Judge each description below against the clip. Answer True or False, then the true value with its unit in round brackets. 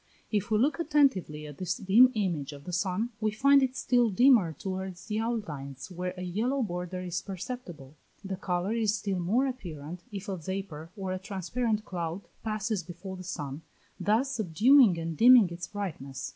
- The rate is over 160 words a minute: True (175 wpm)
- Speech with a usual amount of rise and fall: True (4.3 semitones)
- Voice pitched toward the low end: False (190 Hz)